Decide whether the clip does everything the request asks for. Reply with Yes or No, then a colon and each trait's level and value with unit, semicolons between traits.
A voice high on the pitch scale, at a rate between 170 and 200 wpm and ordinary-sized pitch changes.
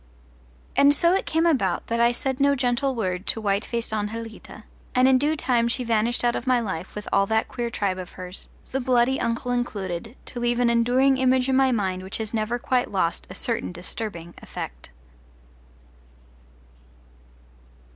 Yes: high, 235 Hz; average, 175 wpm; average, 3.8 semitones